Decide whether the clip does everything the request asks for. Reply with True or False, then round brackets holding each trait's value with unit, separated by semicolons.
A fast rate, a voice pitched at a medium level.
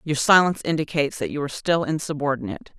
False (170 wpm; 150 Hz)